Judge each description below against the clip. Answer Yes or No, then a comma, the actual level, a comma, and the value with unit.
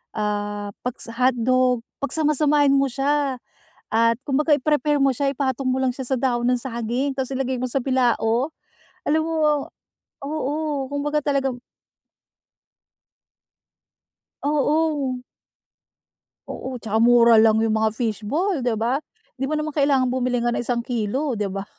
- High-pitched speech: Yes, very high, 260 Hz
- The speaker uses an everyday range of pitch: Yes, average, 3.3 semitones